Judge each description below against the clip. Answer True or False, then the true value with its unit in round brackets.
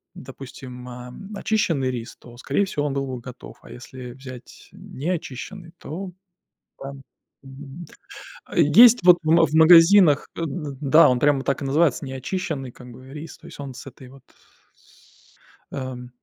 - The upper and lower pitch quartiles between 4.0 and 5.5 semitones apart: True (4.3 semitones)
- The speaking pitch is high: False (140 Hz)